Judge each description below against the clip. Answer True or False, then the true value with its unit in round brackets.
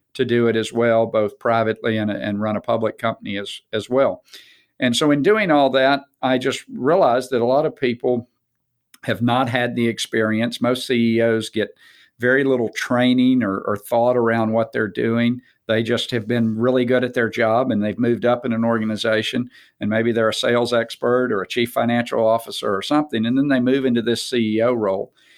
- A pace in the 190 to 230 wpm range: True (200 wpm)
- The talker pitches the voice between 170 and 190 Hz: False (120 Hz)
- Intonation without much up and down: True (1.8 semitones)